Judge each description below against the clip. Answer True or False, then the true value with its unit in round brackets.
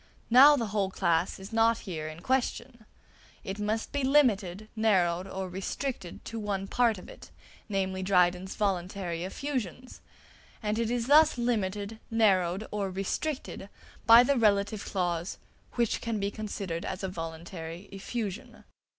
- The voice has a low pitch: False (200 Hz)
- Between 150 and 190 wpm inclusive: False (140 wpm)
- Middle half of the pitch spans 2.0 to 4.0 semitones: True (3.7 semitones)